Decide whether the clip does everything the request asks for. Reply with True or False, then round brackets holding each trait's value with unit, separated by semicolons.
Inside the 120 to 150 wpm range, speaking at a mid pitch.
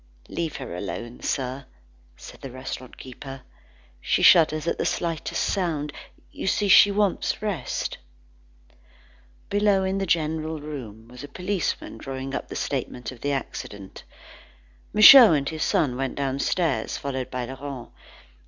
True (140 wpm; 145 Hz)